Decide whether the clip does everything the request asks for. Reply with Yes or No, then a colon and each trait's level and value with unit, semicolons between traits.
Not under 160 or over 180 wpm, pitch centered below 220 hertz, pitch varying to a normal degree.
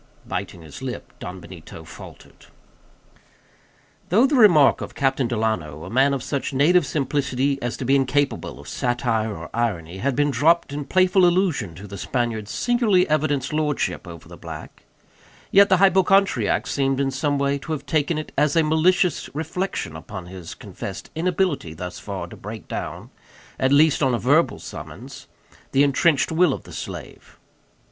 No: average, 165 wpm; medium, 140 Hz; wide, 5.7 semitones